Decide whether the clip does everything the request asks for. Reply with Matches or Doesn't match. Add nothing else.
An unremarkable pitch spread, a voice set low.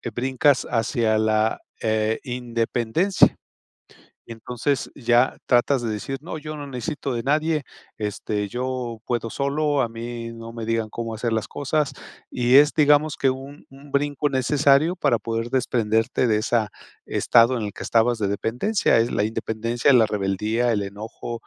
Matches